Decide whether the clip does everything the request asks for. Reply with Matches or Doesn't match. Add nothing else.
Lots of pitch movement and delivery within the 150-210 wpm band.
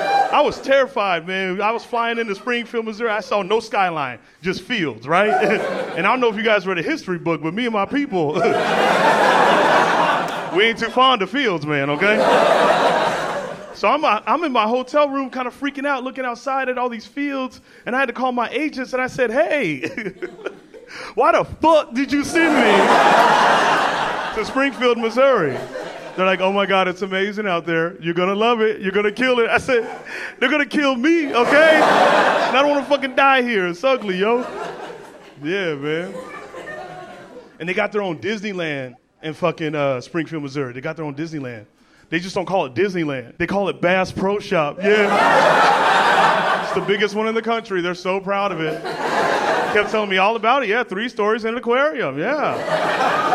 Matches